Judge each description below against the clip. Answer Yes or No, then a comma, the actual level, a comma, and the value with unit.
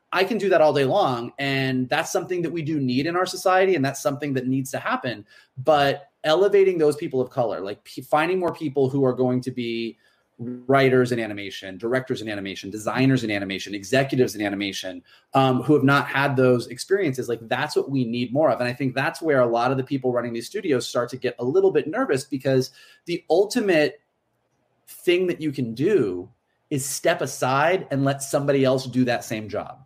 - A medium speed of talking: No, fast, 210 wpm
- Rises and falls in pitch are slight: No, average, 3.4 semitones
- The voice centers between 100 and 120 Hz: No, low, 130 Hz